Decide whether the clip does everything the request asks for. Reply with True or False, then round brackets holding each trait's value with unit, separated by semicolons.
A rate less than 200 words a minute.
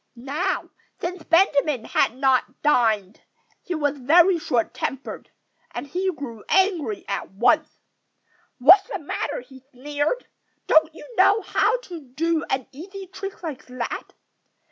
True (140 wpm)